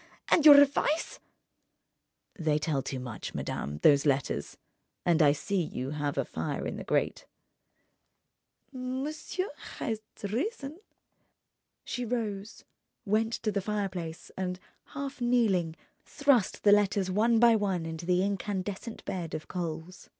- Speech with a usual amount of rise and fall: No, wide, 6.5 semitones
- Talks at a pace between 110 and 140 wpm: Yes, slow, 135 wpm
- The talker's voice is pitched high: Yes, high, 200 Hz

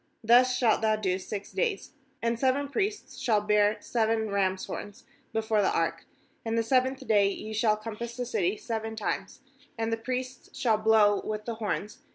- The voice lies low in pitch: No, high, 220 Hz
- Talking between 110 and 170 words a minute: No, average, 180 wpm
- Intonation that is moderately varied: No, narrow, 2.3 semitones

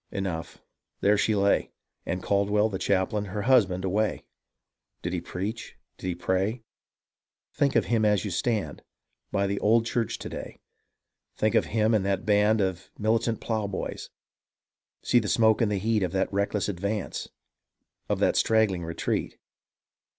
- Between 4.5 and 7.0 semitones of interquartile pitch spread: No, narrow, 2.5 semitones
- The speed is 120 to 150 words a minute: No, average, 160 wpm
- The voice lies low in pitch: Yes, low, 105 Hz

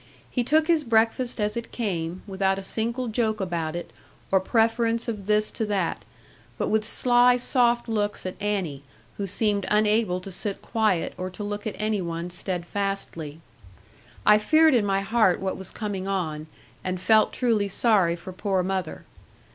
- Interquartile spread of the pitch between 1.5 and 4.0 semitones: Yes, average, 3.4 semitones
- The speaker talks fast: No, average, 170 wpm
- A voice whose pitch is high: Yes, high, 205 Hz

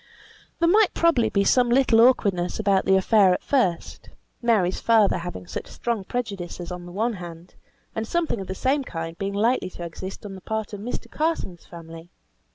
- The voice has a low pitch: No, high, 200 Hz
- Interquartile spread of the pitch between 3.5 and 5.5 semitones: Yes, average, 5.0 semitones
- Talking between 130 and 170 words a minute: No, average, 185 wpm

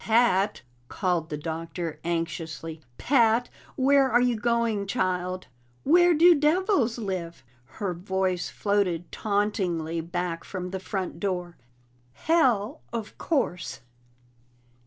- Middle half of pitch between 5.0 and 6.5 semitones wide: Yes, average, 5.3 semitones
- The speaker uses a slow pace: Yes, slow, 110 wpm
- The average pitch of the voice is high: Yes, high, 195 Hz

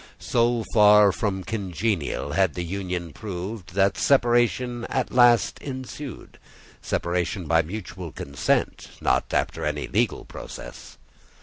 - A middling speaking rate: No, slow, 110 wpm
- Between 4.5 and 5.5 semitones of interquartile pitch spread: Yes, average, 5.1 semitones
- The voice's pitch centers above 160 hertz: No, low, 100 Hz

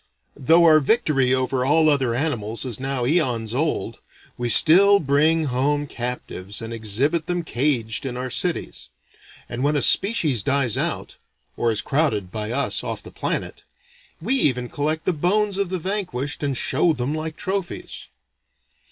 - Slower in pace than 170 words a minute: Yes, average, 160 wpm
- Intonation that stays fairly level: No, average, 4.8 semitones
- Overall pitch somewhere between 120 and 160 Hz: Yes, medium, 140 Hz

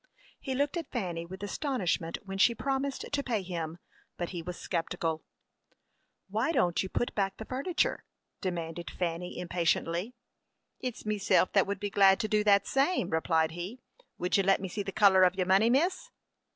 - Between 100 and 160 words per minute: No, average, 180 wpm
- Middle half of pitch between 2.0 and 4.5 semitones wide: No, average, 5.1 semitones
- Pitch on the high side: Yes, high, 195 Hz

